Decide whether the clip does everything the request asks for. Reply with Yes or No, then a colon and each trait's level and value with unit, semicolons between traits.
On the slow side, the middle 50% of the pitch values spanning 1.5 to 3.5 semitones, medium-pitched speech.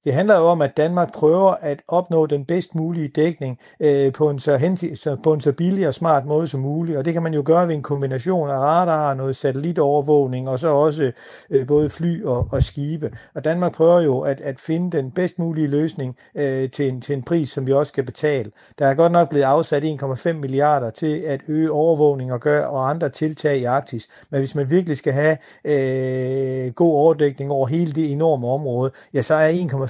No: average, 215 wpm; average, 2.9 semitones; medium, 150 Hz